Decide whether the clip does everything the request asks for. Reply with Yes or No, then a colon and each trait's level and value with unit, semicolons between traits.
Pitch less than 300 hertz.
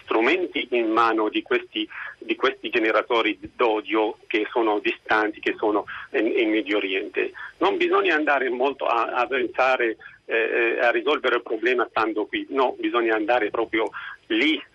No: very high, 360 Hz